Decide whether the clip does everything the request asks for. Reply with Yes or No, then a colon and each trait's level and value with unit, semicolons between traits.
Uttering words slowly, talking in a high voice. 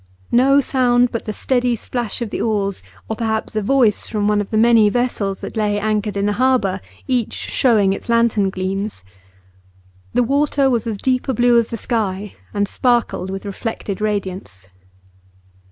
No: average, 170 wpm; high, 220 Hz